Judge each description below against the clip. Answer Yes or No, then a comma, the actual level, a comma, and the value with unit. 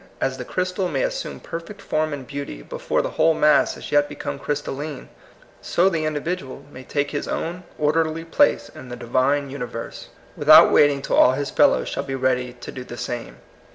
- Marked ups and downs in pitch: No, average, 3.8 semitones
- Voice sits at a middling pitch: Yes, medium, 145 Hz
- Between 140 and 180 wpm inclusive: No, average, 200 wpm